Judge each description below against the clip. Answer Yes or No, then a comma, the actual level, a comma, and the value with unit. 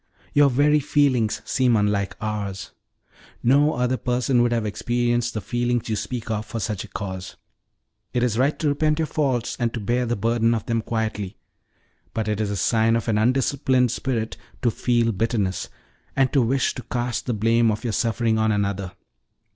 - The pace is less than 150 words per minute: No, average, 185 wpm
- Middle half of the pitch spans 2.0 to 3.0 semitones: Yes, narrow, 2.6 semitones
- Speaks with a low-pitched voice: Yes, low, 115 Hz